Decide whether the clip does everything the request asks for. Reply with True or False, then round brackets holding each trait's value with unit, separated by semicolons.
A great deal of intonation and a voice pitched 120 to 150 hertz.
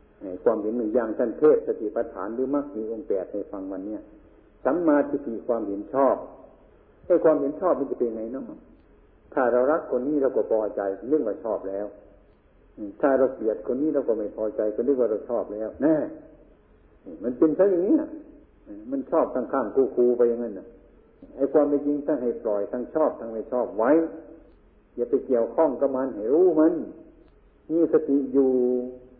True (7.1 semitones; 135 Hz)